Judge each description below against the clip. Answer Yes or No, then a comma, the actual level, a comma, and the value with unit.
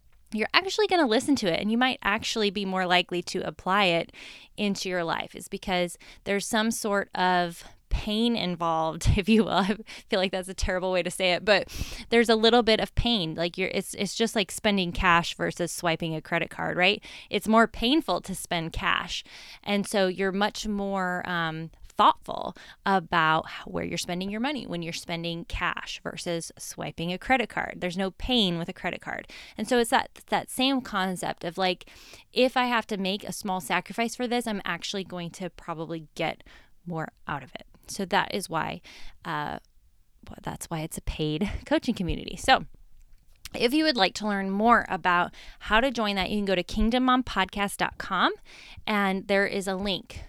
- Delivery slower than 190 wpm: No, average, 195 wpm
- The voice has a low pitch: No, high, 195 Hz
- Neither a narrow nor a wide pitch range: Yes, average, 3.8 semitones